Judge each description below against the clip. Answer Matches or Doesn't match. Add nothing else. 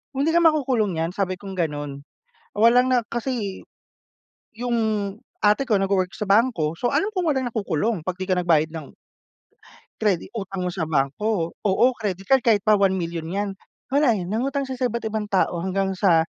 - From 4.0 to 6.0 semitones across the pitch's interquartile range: Matches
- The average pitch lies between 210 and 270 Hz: Doesn't match